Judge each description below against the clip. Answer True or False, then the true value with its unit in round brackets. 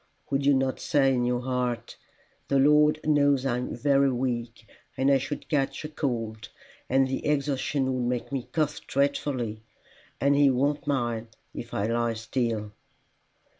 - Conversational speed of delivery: True (155 wpm)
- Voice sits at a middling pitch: False (130 Hz)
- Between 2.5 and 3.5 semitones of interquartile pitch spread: True (2.8 semitones)